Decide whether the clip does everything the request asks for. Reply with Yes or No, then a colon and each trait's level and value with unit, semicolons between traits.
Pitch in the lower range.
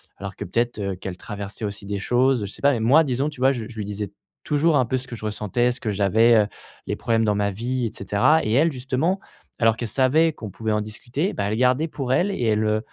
Yes: low, 115 Hz